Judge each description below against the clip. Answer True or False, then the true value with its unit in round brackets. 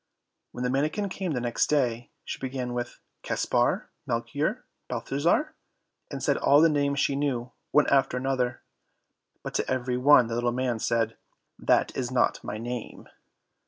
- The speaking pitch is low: True (130 Hz)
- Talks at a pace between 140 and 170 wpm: True (160 wpm)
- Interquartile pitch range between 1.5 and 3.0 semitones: True (2.7 semitones)